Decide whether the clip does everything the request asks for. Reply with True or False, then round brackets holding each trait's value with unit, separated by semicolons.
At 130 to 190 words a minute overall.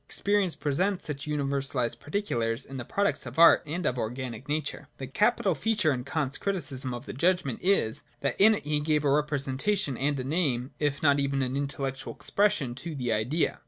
False (200 wpm)